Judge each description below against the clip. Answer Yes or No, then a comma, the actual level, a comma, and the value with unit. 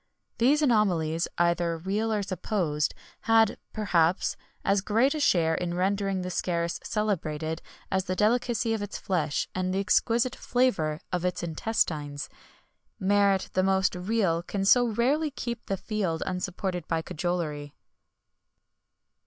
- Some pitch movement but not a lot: Yes, average, 4.2 semitones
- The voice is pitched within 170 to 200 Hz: Yes, high, 190 Hz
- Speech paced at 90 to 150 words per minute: Yes, average, 140 wpm